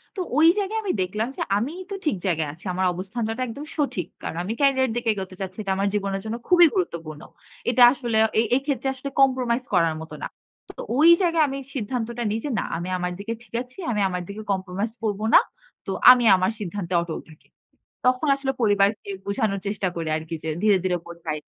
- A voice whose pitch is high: Yes, high, 210 Hz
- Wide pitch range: Yes, wide, 5.7 semitones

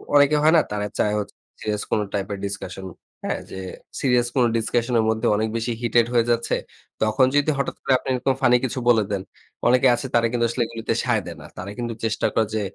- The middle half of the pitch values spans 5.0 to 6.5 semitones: No, average, 2.7 semitones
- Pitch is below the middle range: Yes, low, 115 Hz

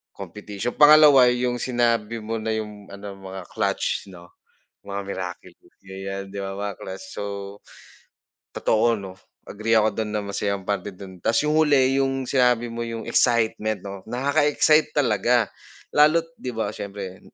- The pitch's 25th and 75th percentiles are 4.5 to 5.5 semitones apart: No, average, 3.8 semitones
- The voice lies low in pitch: Yes, low, 110 Hz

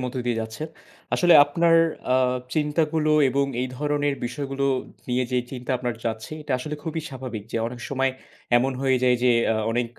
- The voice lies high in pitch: No, low, 135 Hz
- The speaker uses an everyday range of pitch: Yes, average, 3.1 semitones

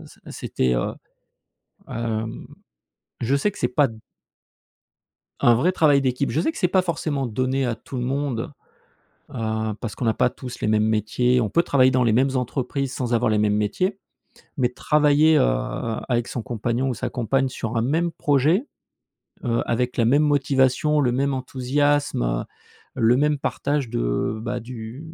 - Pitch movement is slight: No, average, 3.7 semitones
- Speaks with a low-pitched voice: Yes, low, 125 Hz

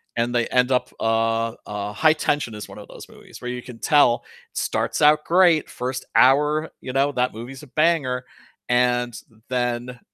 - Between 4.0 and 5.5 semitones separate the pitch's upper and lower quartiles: No, average, 3.4 semitones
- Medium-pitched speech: No, low, 125 Hz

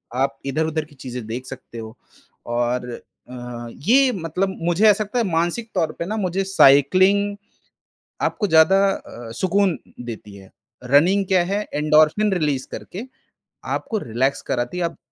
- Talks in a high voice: No, medium, 160 Hz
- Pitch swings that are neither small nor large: No, wide, 7.0 semitones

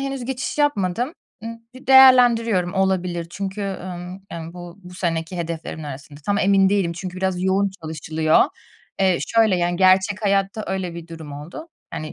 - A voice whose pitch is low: No, medium, 185 Hz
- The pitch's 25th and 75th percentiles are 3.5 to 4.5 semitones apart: No, average, 3.1 semitones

